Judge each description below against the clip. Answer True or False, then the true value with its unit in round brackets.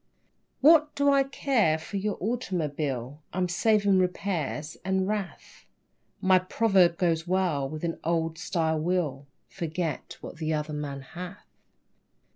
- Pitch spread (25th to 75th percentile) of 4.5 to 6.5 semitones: False (3.9 semitones)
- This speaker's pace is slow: True (130 wpm)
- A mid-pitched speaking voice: True (175 Hz)